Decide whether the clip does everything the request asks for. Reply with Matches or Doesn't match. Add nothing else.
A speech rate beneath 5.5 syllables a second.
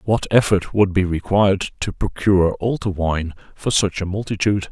Matches